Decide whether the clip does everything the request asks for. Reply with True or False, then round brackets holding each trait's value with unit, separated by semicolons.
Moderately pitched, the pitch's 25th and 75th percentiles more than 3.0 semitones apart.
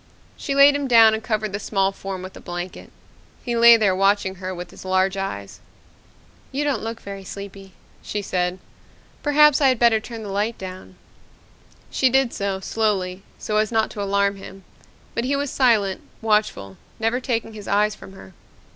False (210 Hz; 3.4 semitones)